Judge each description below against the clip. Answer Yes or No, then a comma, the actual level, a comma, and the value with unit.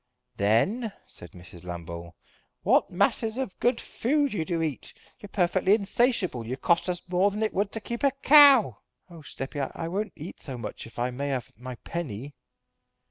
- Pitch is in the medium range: Yes, medium, 170 Hz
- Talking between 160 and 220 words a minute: Yes, average, 180 wpm